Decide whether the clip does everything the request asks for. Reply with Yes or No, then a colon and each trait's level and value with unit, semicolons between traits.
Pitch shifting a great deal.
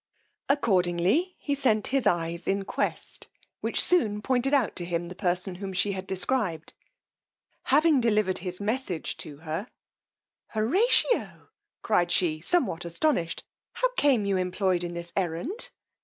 Yes: wide, 7.0 semitones